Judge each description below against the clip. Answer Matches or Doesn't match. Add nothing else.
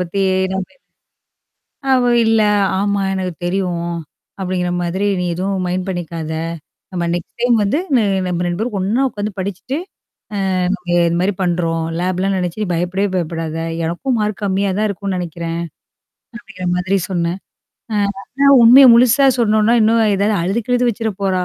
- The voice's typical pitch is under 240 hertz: Matches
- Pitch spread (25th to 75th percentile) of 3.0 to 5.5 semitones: Matches